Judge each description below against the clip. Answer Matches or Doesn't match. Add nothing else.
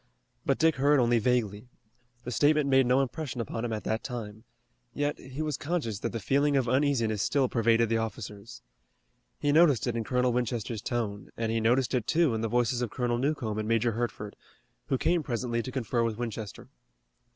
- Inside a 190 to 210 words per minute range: Matches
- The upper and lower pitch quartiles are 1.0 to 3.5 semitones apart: Matches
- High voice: Doesn't match